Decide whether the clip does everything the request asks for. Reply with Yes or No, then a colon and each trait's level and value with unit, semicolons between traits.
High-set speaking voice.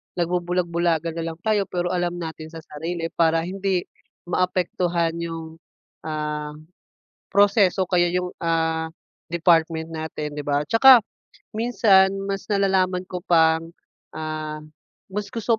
No: medium, 170 Hz